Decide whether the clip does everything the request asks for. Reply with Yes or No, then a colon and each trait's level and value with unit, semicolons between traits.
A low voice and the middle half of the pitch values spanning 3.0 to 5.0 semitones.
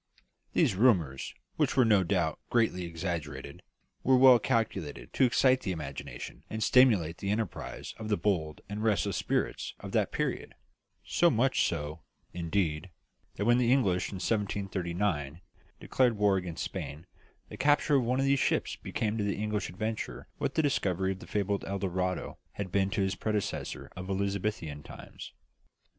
Yes: low, 100 Hz; average, 4.3 semitones